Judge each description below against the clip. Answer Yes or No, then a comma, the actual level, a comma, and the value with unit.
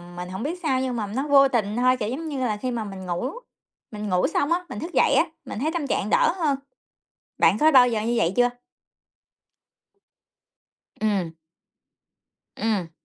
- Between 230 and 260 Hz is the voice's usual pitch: Yes, high, 240 Hz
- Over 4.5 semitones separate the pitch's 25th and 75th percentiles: Yes, average, 5.0 semitones